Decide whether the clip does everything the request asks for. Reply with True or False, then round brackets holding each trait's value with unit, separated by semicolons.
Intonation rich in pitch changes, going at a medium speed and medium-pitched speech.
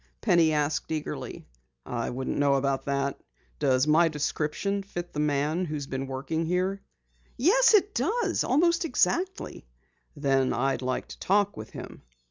True (6.3 semitones; 150 wpm; 150 Hz)